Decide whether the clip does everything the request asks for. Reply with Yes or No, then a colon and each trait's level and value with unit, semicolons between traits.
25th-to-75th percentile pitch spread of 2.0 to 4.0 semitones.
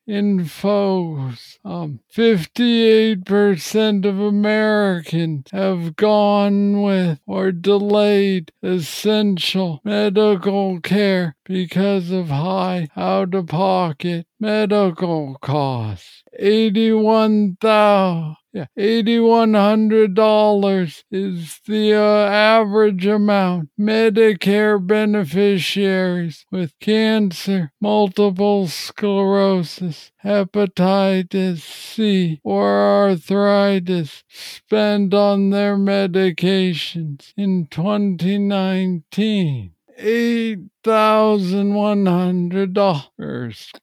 Yes: narrow, 2.5 semitones